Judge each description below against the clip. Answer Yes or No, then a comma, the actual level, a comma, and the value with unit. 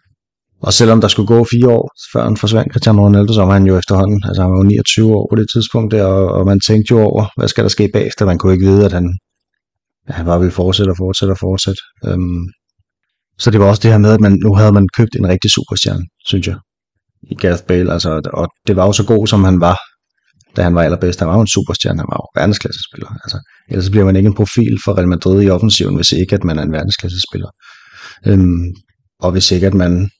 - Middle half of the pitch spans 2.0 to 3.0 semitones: Yes, average, 2.7 semitones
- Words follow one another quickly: Yes, fast, 245 wpm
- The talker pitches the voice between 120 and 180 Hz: No, low, 100 Hz